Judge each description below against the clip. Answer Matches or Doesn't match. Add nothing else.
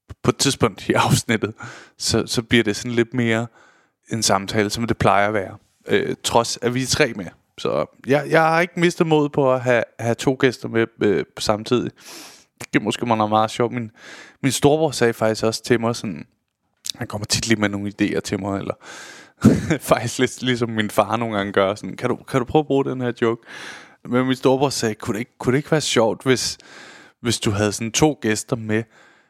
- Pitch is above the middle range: Doesn't match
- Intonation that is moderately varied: Matches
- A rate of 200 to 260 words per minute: Matches